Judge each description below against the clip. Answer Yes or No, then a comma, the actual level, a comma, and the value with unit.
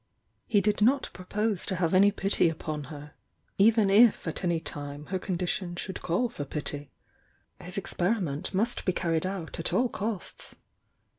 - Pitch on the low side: No, medium, 185 Hz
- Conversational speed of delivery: Yes, average, 165 wpm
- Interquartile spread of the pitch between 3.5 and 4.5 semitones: Yes, average, 4.1 semitones